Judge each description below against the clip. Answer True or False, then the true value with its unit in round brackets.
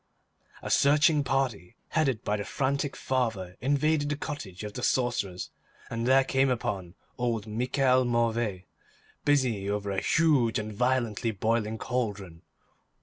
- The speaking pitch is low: True (120 Hz)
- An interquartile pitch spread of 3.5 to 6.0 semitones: True (4.4 semitones)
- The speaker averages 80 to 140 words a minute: True (135 wpm)